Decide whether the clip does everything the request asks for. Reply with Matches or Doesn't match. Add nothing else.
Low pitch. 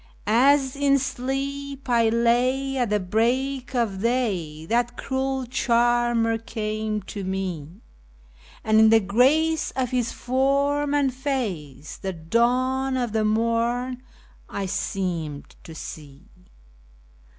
Doesn't match